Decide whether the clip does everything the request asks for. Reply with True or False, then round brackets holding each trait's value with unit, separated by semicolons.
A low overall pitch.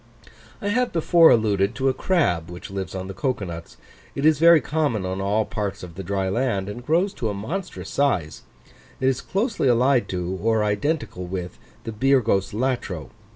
True (110 Hz)